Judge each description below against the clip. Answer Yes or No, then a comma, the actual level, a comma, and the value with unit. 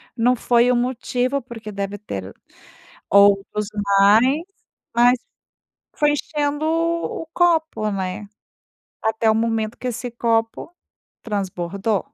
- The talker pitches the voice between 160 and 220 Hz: No, high, 230 Hz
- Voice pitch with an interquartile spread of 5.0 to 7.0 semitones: No, average, 3.8 semitones